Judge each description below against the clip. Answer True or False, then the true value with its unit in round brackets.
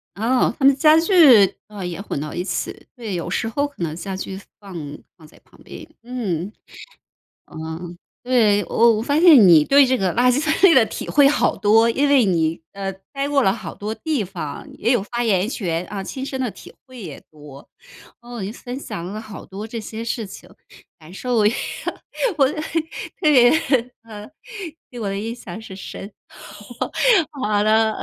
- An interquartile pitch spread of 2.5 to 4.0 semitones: False (4.8 semitones)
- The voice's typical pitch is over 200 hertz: True (220 Hz)